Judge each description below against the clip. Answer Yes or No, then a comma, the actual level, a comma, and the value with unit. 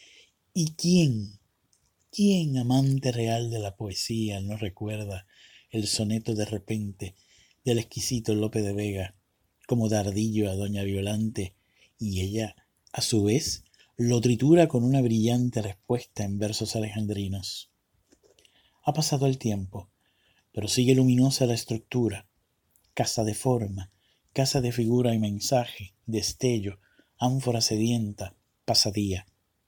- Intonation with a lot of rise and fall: No, average, 3.2 semitones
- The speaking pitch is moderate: No, low, 110 Hz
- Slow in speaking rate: Yes, slow, 120 wpm